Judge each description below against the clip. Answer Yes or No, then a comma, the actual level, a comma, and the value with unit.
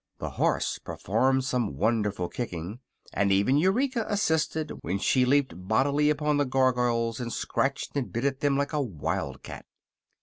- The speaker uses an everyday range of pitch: Yes, average, 4.6 semitones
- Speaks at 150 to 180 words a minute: Yes, average, 160 wpm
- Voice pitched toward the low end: Yes, low, 130 Hz